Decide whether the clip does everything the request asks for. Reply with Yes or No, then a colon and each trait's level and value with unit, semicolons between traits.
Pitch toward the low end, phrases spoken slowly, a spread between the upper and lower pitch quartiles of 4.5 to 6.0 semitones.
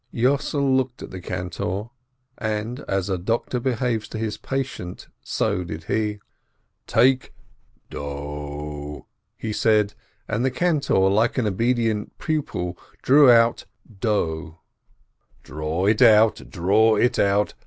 Yes: low, 110 Hz; slow, 120 wpm; average, 5.2 semitones